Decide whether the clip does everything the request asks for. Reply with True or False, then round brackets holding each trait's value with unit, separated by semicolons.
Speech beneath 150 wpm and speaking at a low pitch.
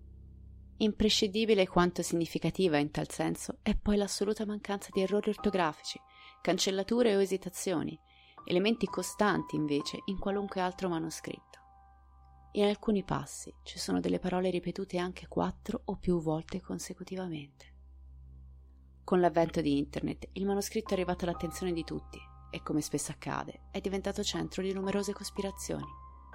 False (130 wpm; 180 Hz)